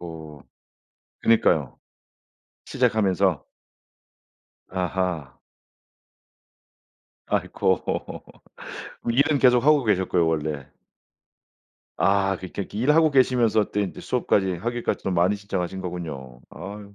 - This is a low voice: Yes, very low, 95 Hz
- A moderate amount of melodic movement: Yes, average, 5.0 semitones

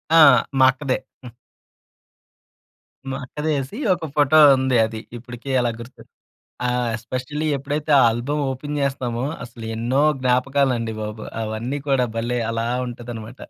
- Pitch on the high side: No, low, 125 Hz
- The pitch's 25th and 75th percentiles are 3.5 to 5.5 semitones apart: No, average, 2.8 semitones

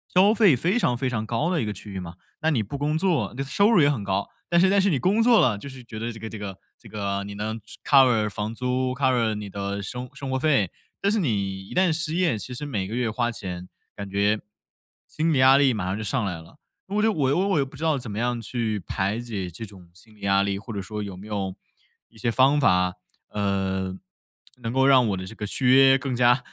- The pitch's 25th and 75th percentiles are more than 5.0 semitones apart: Yes, wide, 5.5 semitones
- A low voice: Yes, low, 115 Hz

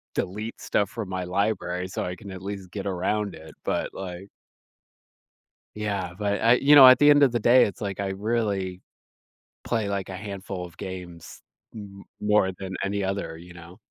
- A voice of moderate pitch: No, low, 100 Hz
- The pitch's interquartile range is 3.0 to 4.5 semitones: No, narrow, 2.4 semitones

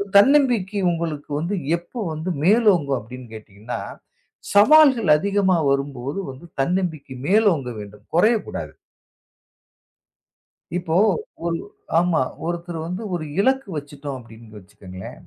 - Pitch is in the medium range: Yes, medium, 165 Hz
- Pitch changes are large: Yes, wide, 6.9 semitones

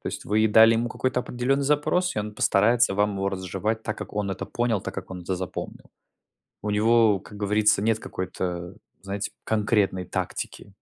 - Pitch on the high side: No, low, 105 Hz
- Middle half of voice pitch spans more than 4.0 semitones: No, average, 2.7 semitones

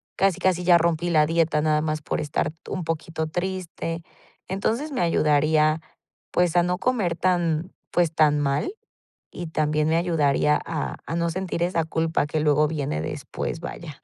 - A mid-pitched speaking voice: Yes, medium, 165 Hz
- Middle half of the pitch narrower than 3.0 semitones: Yes, narrow, 2.4 semitones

